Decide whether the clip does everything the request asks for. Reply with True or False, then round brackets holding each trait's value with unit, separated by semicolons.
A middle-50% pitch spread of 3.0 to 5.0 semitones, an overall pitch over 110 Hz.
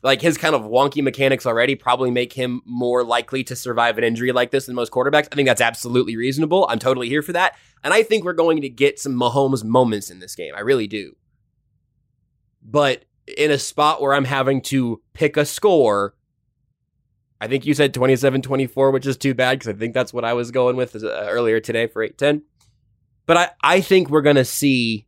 False (2.6 semitones; 130 Hz)